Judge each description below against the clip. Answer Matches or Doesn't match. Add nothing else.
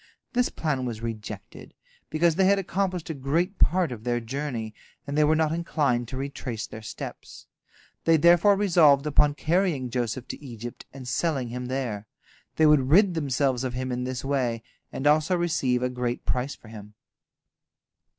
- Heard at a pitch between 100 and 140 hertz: Matches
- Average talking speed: Matches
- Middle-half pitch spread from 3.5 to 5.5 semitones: Matches